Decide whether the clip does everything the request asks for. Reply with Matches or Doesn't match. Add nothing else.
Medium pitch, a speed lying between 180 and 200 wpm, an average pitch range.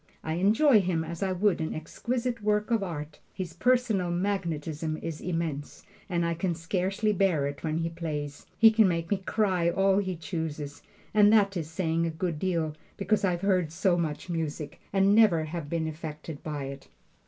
Matches